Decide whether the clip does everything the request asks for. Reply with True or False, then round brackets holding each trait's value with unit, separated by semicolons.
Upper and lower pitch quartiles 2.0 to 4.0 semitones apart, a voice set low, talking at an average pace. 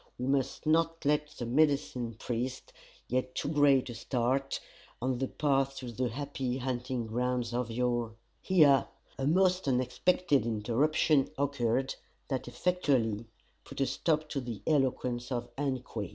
True (2.9 semitones; 130 Hz; 145 wpm)